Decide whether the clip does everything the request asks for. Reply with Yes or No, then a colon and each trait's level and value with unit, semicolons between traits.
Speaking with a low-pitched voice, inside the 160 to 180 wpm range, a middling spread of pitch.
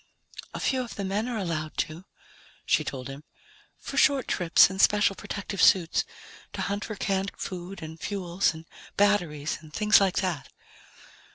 No: high, 190 Hz; average, 165 wpm; average, 4.0 semitones